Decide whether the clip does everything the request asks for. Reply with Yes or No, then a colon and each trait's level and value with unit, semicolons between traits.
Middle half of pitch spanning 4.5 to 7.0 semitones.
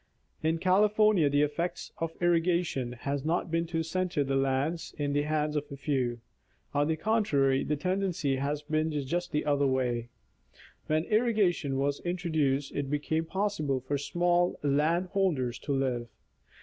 No: average, 3.8 semitones